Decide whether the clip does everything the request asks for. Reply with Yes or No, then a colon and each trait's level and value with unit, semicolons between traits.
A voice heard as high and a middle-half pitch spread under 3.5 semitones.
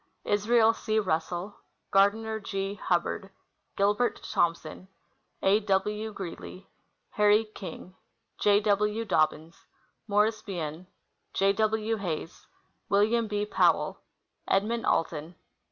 Yes: high, 205 Hz; average, 2.7 semitones